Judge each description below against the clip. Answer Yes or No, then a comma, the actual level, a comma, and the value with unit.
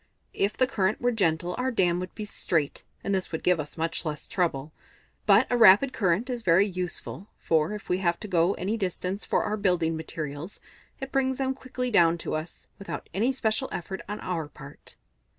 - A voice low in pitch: No, medium, 185 Hz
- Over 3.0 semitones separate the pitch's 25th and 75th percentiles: Yes, average, 4.7 semitones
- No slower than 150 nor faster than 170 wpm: No, average, 200 wpm